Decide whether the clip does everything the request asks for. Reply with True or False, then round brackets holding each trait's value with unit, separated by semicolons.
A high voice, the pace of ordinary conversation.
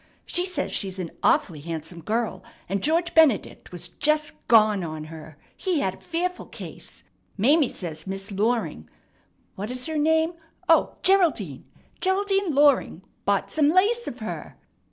True (240 Hz; 150 wpm)